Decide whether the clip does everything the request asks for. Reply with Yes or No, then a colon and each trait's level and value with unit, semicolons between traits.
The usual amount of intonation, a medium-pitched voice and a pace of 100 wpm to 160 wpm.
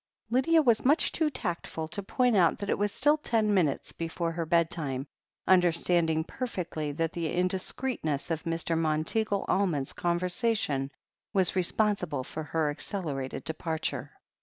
Yes: average, 4.5 semitones; medium, 175 Hz; average, 140 wpm